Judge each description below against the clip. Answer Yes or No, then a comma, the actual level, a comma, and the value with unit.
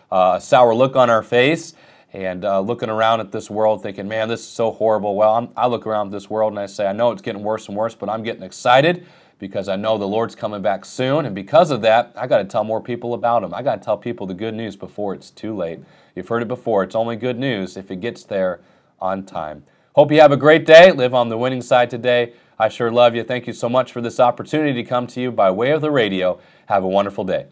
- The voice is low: Yes, low, 115 Hz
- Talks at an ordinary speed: No, fast, 270 wpm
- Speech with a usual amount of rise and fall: Yes, average, 3.0 semitones